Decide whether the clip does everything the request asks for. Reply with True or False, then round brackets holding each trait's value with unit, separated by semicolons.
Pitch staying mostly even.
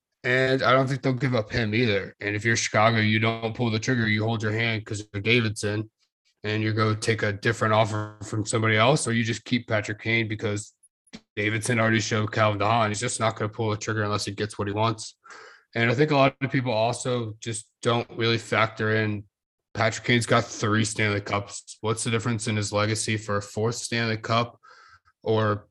True (1.7 semitones)